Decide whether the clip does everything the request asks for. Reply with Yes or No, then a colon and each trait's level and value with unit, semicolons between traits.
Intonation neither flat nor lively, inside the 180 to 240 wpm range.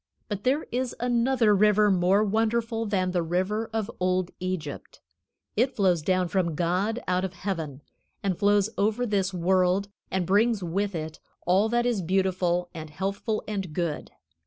No: average, 3.2 semitones; average, 160 wpm